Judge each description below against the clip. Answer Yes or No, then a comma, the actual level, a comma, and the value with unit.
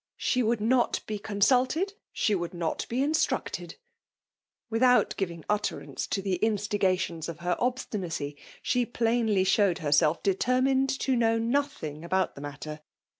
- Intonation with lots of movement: Yes, wide, 6.1 semitones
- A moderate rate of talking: Yes, average, 155 wpm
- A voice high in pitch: Yes, high, 210 Hz